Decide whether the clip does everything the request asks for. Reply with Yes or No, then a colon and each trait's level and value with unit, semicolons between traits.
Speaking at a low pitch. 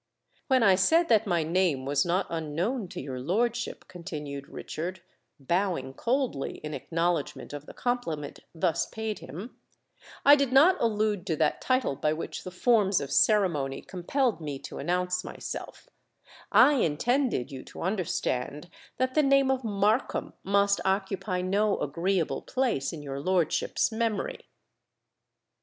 No: medium, 185 Hz